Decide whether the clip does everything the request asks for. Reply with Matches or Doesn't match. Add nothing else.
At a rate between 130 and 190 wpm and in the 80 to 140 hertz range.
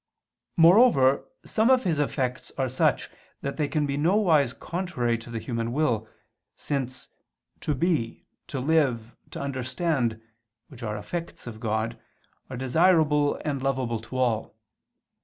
Matches